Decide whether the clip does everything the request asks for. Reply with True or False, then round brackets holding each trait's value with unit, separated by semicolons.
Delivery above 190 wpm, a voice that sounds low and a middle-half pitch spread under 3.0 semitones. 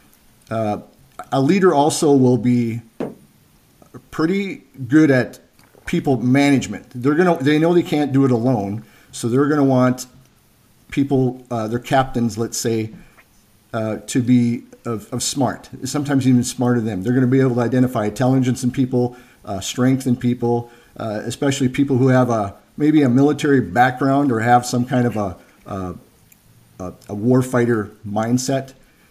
False (160 wpm; 125 Hz; 2.5 semitones)